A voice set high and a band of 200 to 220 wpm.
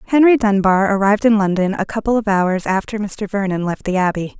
Yes: high, 200 Hz; fast, 205 wpm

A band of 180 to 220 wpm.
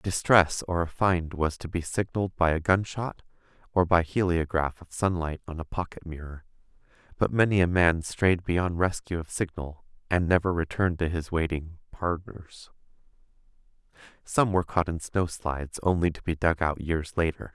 No: average, 165 wpm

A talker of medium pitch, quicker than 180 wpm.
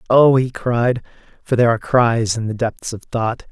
No: low, 120 Hz; fast, 205 wpm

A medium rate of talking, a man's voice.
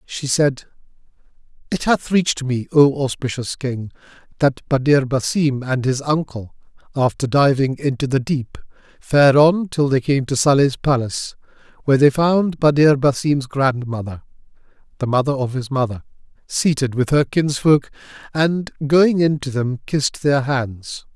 Yes: average, 145 wpm; male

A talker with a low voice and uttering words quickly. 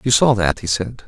Yes: low, 110 Hz; fast, 280 wpm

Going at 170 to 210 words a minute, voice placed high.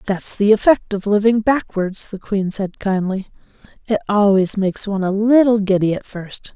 Yes: average, 175 wpm; high, 205 Hz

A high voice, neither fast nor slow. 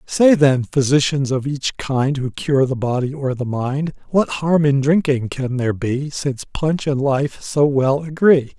No: medium, 140 Hz; average, 190 wpm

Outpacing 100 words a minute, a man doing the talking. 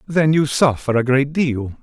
Yes: average, 200 wpm; male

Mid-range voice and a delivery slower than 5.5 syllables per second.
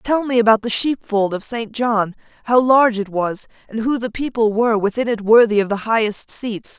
No: high, 225 Hz; 5.2 syllables/s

